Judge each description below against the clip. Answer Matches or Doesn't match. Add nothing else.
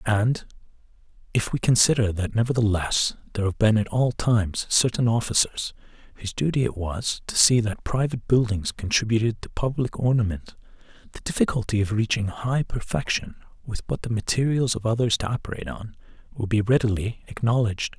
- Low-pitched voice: Matches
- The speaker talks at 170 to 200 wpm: Doesn't match